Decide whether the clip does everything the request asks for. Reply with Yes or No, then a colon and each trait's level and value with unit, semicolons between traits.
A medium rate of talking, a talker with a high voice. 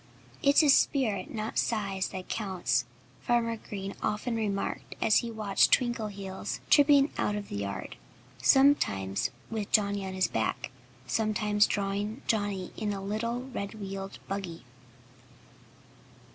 No: slow, 125 wpm; high, 205 Hz